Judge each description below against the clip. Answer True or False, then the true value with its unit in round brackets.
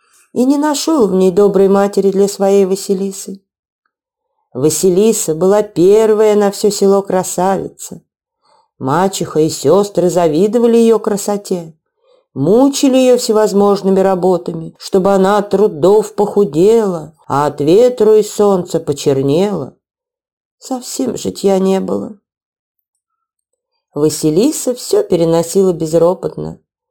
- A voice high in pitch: True (200 Hz)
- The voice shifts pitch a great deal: False (3.5 semitones)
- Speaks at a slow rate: True (105 wpm)